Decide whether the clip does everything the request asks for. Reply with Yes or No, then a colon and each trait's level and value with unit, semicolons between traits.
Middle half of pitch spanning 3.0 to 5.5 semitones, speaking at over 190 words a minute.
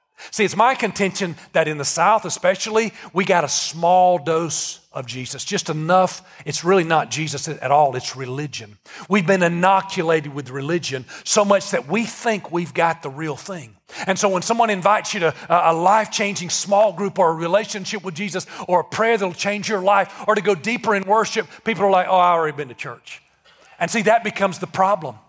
Yes: average, 4.2 semitones; average, 200 wpm